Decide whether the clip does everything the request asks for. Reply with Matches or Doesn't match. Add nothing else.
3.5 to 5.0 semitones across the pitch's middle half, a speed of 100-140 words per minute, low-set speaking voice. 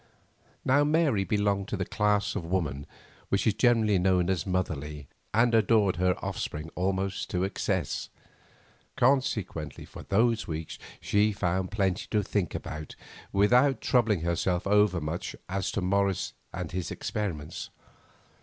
Doesn't match